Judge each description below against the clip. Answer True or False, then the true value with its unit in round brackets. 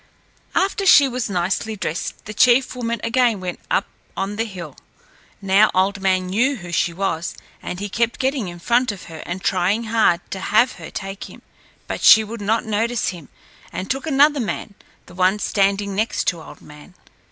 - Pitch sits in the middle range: False (205 Hz)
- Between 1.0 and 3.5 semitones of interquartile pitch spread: False (4.0 semitones)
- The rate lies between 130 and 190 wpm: True (185 wpm)